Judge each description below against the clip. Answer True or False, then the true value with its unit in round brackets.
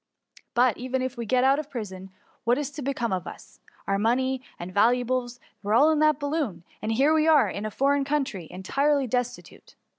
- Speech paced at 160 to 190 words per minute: False (200 wpm)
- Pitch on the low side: False (255 Hz)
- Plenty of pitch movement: False (4.4 semitones)